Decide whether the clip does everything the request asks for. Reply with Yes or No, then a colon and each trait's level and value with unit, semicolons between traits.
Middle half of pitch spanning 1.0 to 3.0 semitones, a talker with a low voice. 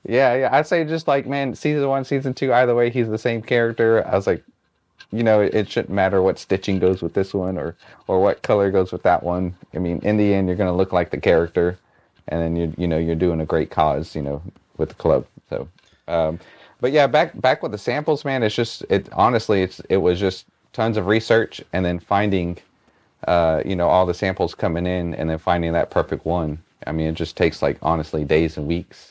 No: average, 4.8 semitones; very low, 95 Hz